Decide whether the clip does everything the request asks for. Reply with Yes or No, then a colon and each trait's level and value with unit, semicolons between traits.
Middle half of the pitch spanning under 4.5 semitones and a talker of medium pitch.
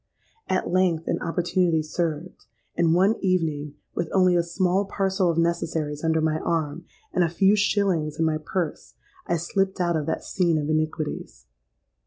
Yes: average, 2.7 semitones; medium, 170 Hz